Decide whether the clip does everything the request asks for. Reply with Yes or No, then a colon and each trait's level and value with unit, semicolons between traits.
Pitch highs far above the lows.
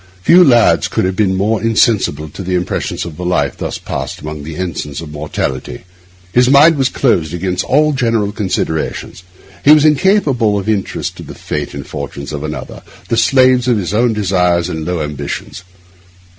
Yes: wide, 7.4 semitones